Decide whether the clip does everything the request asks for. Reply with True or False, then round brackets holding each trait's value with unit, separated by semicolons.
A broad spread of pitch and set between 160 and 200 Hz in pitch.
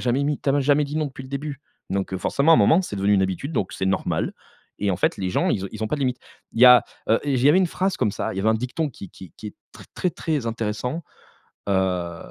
False (6.6 semitones; 125 Hz)